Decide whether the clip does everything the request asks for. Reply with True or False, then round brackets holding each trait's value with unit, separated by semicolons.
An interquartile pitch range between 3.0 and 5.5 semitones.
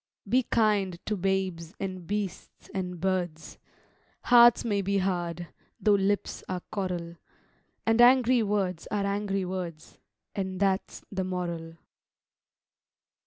False (2.4 semitones)